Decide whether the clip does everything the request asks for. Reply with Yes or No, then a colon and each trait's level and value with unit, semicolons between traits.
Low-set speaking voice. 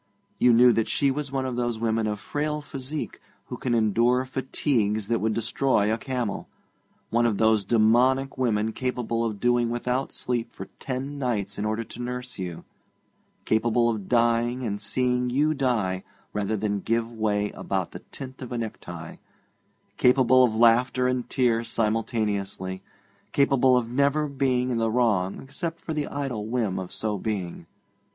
Yes: low, 120 Hz